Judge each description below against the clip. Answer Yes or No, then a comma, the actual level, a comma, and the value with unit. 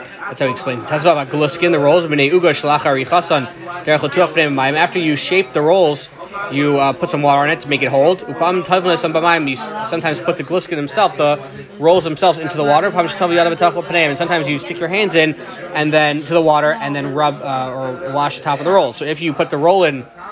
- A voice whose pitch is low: No, medium, 160 Hz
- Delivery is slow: No, average, 200 wpm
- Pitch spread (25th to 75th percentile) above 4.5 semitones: No, average, 3.2 semitones